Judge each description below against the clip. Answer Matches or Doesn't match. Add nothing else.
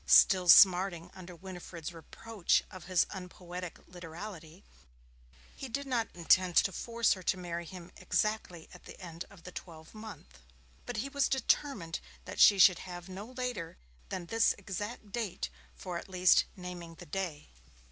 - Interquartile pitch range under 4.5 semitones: Matches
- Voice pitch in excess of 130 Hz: Matches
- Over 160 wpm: Doesn't match